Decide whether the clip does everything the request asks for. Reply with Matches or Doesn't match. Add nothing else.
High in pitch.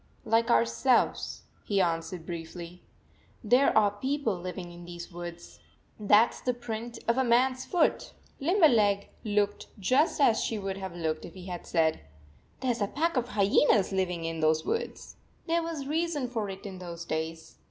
Matches